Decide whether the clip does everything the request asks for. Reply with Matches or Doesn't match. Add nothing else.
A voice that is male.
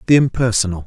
Matches